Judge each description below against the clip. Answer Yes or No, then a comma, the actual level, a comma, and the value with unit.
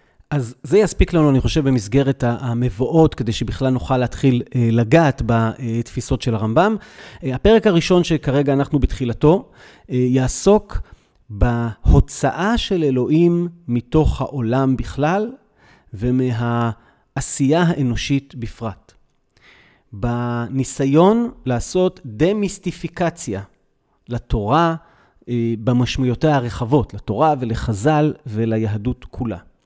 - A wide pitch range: No, average, 4.9 semitones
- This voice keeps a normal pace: No, slow, 85 wpm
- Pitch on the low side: Yes, low, 130 Hz